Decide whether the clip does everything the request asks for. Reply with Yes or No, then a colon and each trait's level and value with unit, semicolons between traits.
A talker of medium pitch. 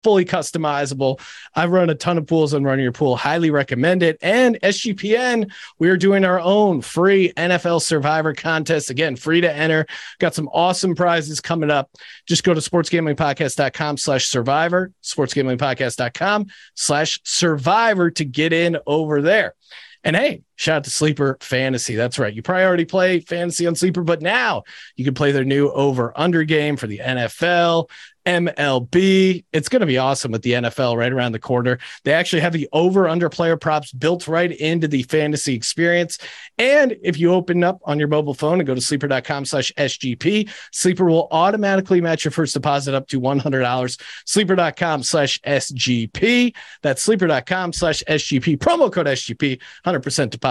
Yes: medium, 155 Hz